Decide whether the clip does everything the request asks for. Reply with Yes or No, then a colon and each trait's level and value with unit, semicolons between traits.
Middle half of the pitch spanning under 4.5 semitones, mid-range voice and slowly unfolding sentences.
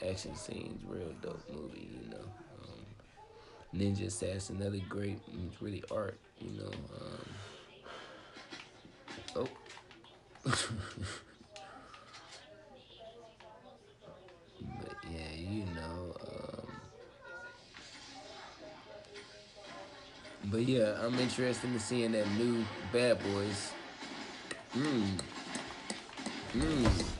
No: average, 4.0 semitones; low, 105 Hz; slow, 80 wpm